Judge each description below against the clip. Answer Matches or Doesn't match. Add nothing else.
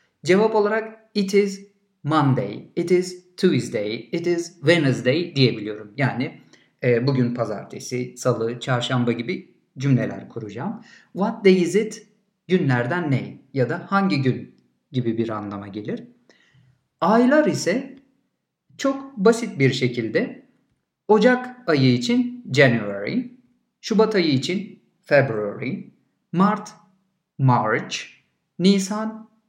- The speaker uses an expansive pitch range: Matches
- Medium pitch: Matches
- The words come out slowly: Doesn't match